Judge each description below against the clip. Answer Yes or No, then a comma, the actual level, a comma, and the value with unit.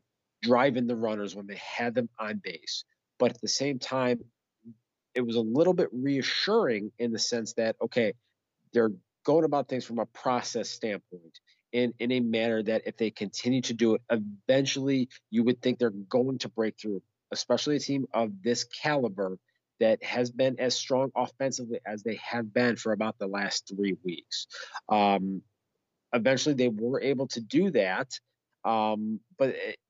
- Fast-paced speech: No, average, 175 wpm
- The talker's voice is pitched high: No, low, 120 Hz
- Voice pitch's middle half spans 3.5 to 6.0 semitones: No, average, 2.7 semitones